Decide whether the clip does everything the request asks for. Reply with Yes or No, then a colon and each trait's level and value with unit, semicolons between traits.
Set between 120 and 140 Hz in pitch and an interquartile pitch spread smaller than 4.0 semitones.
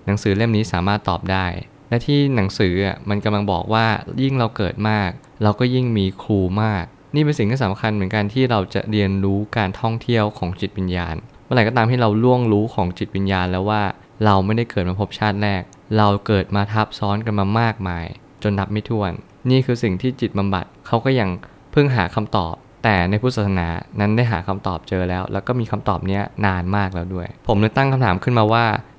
No: low, 105 Hz; average, 3.0 semitones